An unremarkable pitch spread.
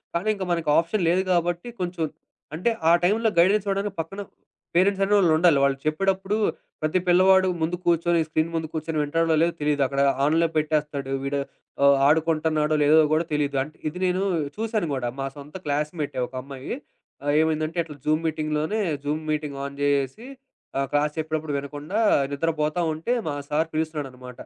Yes: average, 3.0 semitones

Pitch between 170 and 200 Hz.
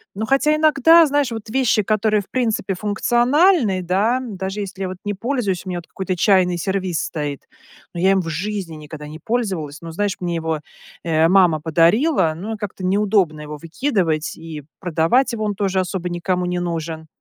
Yes: high, 190 Hz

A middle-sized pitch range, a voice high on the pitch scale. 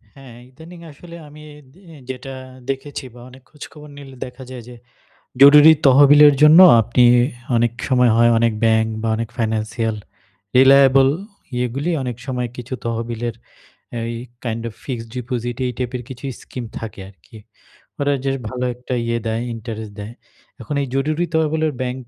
No: average, 3.2 semitones; low, 125 Hz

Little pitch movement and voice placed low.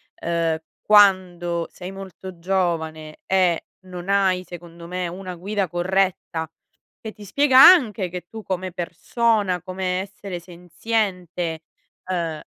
No: narrow, 2.2 semitones; medium, 180 Hz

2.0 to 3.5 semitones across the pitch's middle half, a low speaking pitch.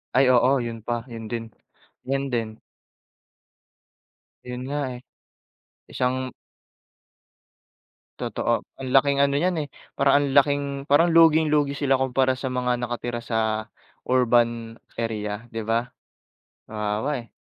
Yes: average, 3.2 semitones; low, 125 Hz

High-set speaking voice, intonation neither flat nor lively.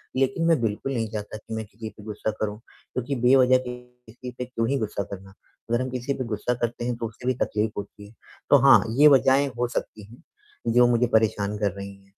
No: low, 115 Hz; average, 3.1 semitones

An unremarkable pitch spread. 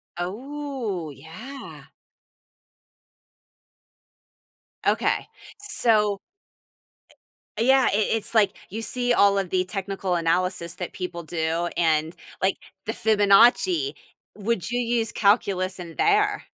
Yes: average, 5.0 semitones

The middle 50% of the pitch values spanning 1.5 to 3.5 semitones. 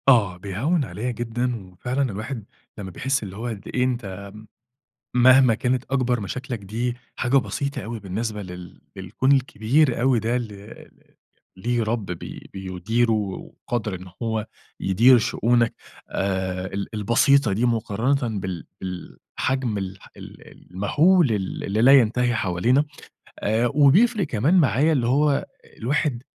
No: average, 4.5 semitones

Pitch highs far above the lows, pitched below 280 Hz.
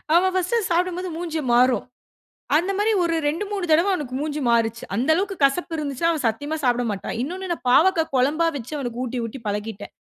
No: wide, 6.1 semitones; very high, 305 Hz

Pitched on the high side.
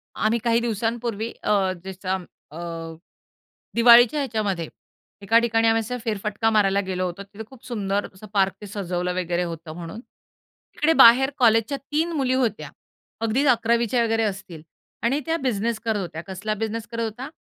Yes: high, 220 Hz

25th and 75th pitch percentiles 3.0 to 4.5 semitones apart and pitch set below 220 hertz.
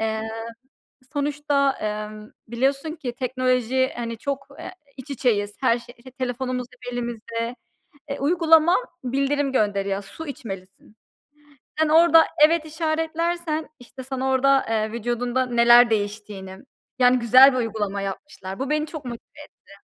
No: average, 4.1 semitones; very high, 250 Hz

